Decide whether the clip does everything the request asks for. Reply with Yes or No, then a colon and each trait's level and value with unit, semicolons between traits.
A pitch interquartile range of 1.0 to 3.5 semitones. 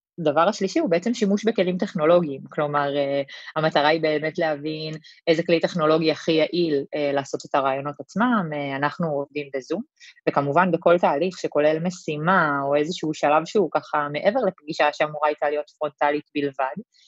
Yes: average, 3.2 semitones